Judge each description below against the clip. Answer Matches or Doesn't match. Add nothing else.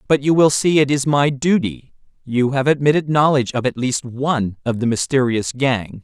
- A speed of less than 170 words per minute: Doesn't match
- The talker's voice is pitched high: Doesn't match